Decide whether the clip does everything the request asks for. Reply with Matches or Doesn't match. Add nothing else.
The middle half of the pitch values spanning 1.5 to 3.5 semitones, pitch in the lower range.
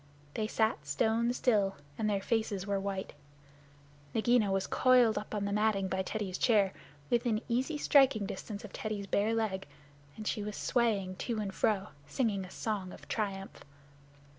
Doesn't match